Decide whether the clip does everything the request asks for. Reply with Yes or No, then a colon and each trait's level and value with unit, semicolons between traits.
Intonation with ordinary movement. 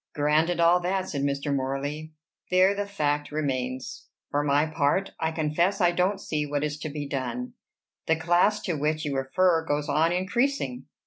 Yes: average, 3.6 semitones